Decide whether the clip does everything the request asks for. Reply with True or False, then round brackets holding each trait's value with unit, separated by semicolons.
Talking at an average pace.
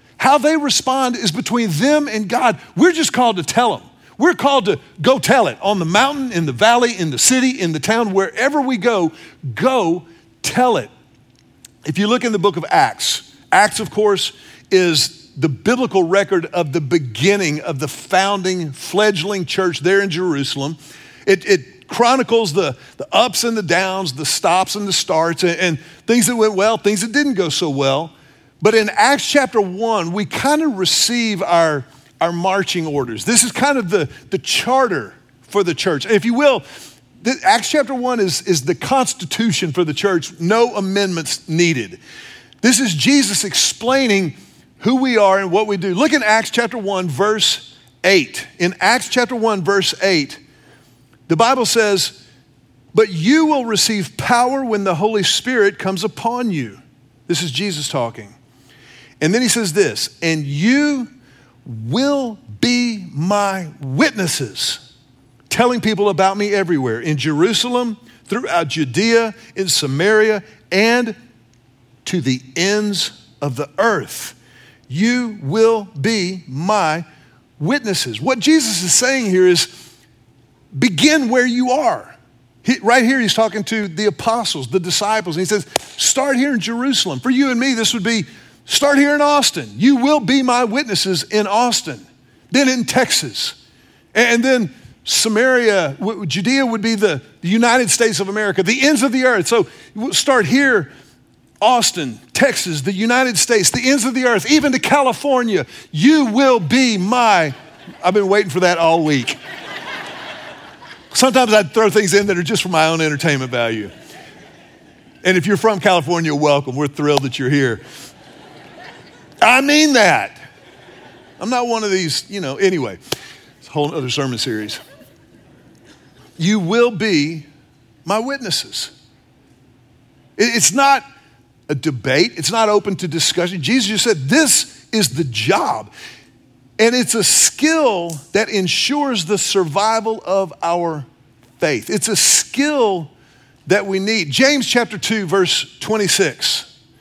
True (155 wpm)